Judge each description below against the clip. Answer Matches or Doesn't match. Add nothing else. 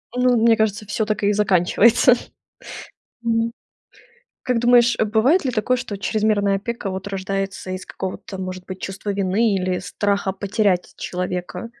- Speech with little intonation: Doesn't match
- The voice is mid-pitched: Doesn't match